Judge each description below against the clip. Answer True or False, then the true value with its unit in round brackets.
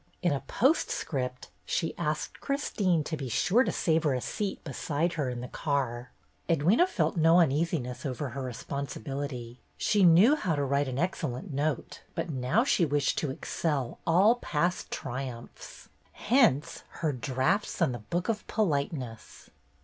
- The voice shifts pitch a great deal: False (4.9 semitones)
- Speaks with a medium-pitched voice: True (150 Hz)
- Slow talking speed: False (165 wpm)